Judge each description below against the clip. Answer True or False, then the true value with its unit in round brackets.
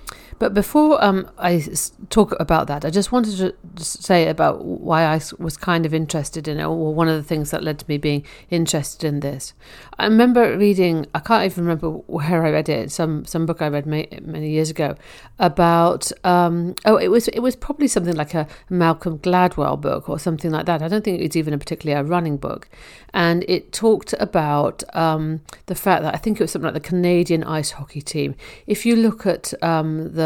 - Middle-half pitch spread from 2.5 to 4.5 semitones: True (2.9 semitones)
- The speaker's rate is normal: False (210 wpm)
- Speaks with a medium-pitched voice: True (165 Hz)